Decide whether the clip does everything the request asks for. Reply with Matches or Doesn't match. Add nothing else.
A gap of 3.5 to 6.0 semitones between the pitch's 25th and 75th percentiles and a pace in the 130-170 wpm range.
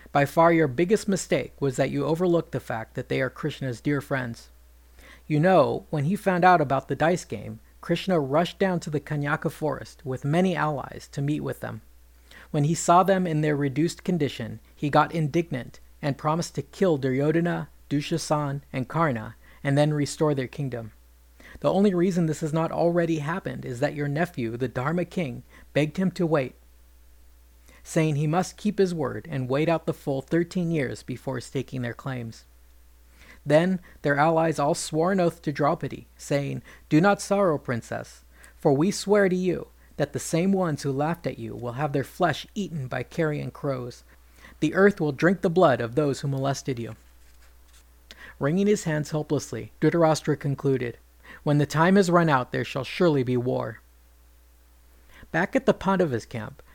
Doesn't match